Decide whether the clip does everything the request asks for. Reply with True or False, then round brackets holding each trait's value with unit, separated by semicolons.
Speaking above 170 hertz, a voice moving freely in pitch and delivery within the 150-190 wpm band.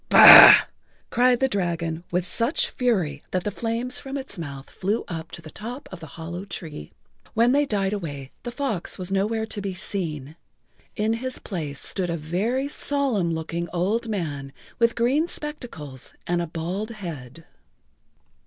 True (190 Hz; 6.0 semitones; 160 wpm)